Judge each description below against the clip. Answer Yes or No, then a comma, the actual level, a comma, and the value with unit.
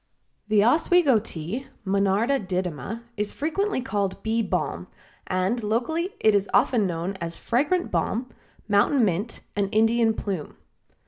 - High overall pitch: Yes, high, 215 Hz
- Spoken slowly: Yes, slow, 130 wpm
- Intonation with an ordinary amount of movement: Yes, average, 4.3 semitones